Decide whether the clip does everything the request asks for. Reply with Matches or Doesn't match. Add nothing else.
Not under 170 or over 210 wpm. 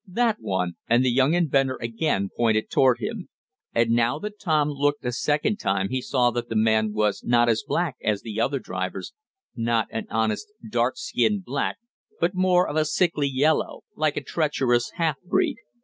Matches